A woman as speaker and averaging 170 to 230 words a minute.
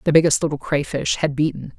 Yes: female; average, 200 wpm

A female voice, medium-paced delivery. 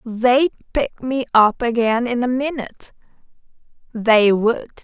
No: female; slow, 125 wpm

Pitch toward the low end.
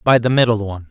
Yes: low, 110 Hz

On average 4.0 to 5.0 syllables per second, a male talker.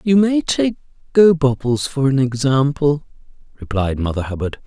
Yes: 4.7 syllables/s; male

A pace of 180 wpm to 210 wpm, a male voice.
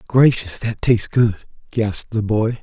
No: average, 160 wpm; male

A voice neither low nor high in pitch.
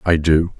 No: very low, 80 Hz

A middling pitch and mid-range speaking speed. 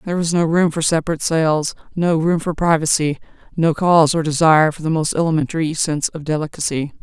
Yes: medium, 160 Hz; average, 190 wpm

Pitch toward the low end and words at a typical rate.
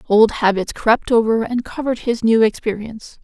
No: high, 225 Hz; average, 165 wpm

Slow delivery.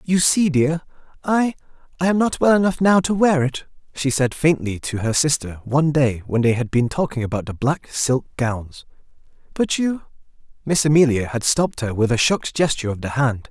No: average, 195 wpm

